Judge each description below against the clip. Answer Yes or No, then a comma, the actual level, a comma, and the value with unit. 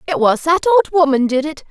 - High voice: Yes, very high, 300 Hz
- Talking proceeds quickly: Yes, fast, 245 wpm